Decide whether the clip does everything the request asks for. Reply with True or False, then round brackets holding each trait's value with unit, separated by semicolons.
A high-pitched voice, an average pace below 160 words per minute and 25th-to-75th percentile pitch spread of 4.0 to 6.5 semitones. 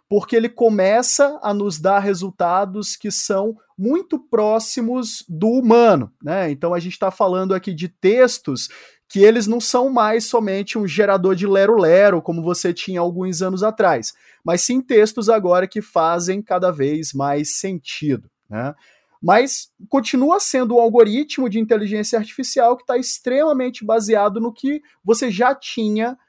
True (215 Hz; 150 wpm; 4.4 semitones)